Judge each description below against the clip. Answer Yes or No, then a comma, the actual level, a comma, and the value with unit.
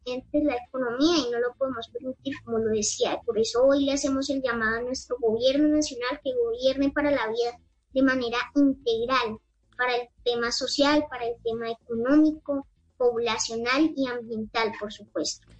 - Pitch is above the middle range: Yes, very high, 250 Hz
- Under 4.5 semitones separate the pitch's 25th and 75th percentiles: Yes, average, 3.1 semitones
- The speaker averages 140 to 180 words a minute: Yes, average, 165 wpm